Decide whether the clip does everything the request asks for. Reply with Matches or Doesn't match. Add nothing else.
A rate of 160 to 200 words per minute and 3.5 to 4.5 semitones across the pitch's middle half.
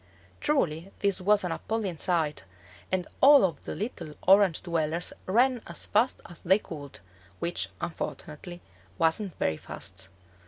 Doesn't match